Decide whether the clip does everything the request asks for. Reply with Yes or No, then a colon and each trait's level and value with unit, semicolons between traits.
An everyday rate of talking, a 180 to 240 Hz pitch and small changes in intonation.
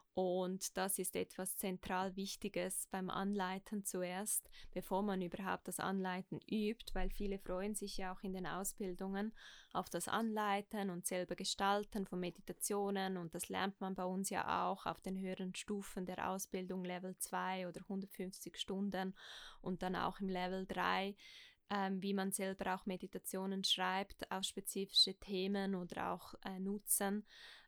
Yes: average, 155 wpm; high, 190 Hz; narrow, 1.2 semitones